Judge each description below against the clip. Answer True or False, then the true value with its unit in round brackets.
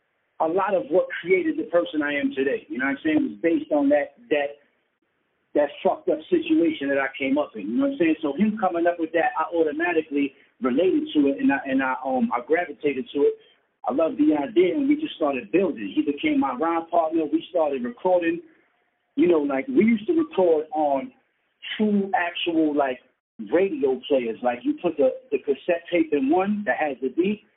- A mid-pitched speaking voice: True (175 Hz)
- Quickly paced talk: True (210 wpm)